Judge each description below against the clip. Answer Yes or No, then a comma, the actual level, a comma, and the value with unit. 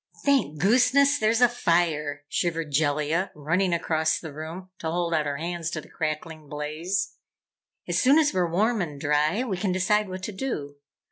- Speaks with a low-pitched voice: No, medium, 170 Hz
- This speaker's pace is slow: No, average, 180 wpm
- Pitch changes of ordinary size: Yes, average, 4.6 semitones